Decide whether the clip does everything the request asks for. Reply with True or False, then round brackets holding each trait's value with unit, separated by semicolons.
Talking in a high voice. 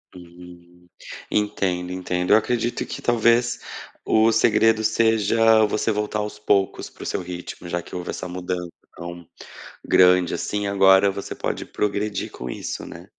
False (100 Hz)